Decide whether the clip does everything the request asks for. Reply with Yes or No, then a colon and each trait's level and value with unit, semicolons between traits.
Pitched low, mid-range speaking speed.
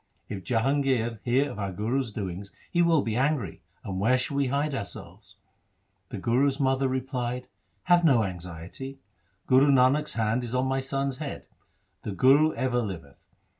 Yes: low, 125 Hz; average, 170 wpm